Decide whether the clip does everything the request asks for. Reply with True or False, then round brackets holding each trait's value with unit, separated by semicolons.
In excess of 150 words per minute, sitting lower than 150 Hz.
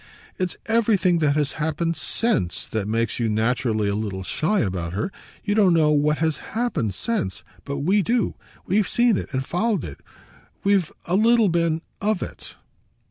False (170 wpm; 160 Hz)